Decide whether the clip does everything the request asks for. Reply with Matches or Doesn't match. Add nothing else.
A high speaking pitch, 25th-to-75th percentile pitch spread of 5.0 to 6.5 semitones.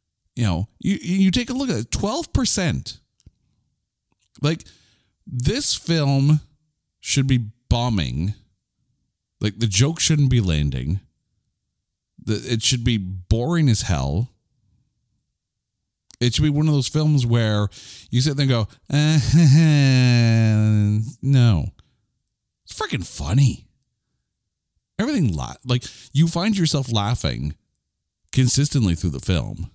Doesn't match